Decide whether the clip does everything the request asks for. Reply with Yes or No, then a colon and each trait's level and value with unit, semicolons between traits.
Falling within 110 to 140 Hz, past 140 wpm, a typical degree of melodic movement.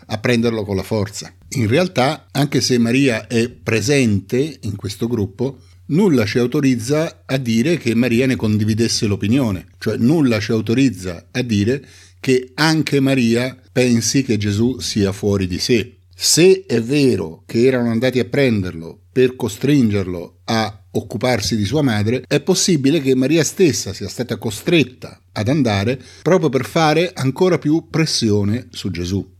Yes: low, 120 Hz; average, 150 wpm; average, 4.4 semitones